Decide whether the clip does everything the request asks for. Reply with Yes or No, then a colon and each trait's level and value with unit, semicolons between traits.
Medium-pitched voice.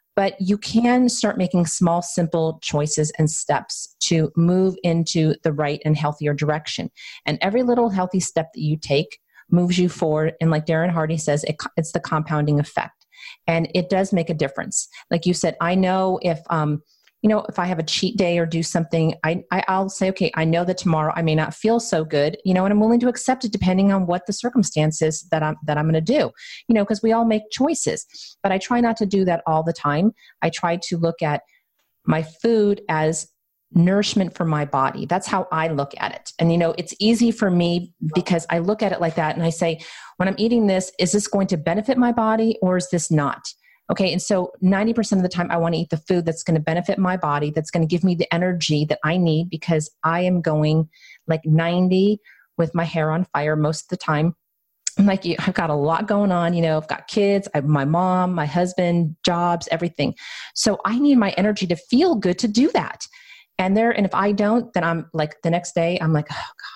Yes: medium, 175 Hz